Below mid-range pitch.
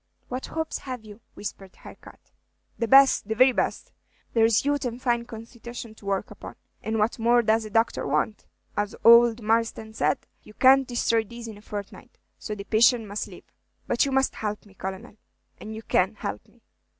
No: high, 225 Hz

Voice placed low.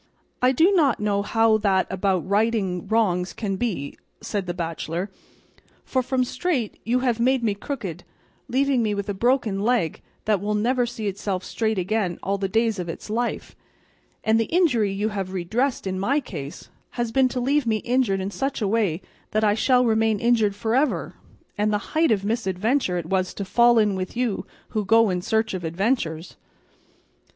No: high, 215 Hz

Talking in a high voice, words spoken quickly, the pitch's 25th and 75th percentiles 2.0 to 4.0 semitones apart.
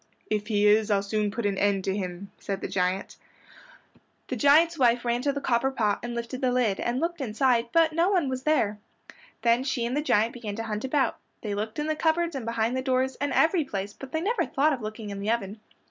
No: high, 235 Hz; fast, 240 wpm; average, 5.0 semitones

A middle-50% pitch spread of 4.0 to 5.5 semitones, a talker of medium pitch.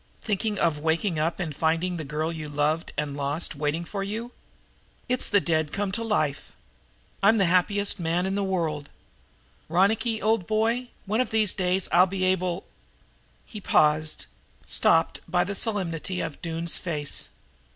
Yes: average, 4.3 semitones; medium, 180 Hz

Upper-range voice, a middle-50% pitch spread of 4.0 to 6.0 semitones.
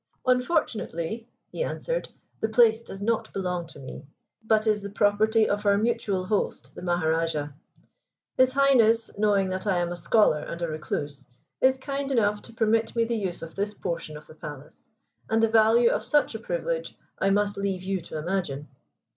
Yes: high, 205 Hz; average, 4.5 semitones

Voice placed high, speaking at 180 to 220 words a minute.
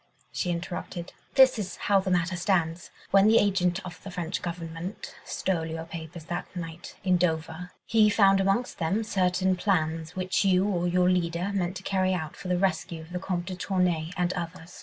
No: medium, 180 Hz; average, 190 wpm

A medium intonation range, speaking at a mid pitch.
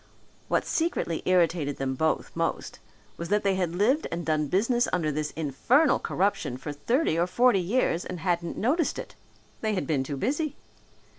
No: wide, 6.8 semitones; medium, 180 Hz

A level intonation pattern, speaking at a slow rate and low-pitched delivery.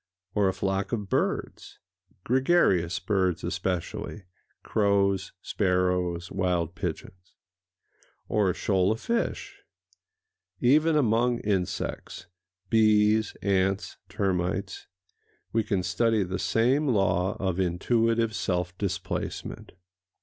No: average, 3.2 semitones; slow, 90 wpm; very low, 95 Hz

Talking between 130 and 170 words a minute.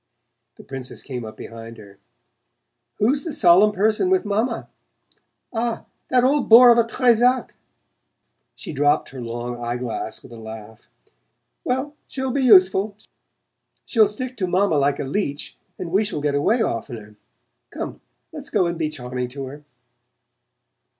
Yes: average, 150 wpm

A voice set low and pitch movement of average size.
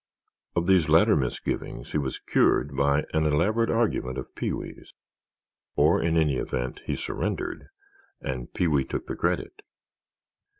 Yes: very low, 75 Hz; average, 4.6 semitones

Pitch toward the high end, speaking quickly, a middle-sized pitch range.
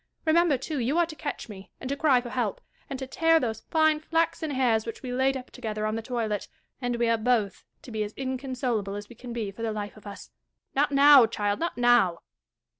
Yes: high, 245 Hz; fast, 230 wpm; average, 4.2 semitones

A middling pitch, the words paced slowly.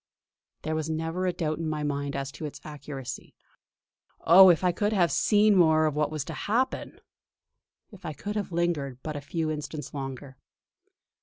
No: medium, 155 Hz; average, 180 wpm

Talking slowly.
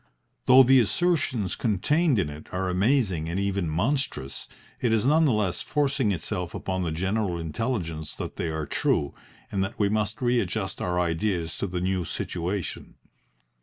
No: average, 165 wpm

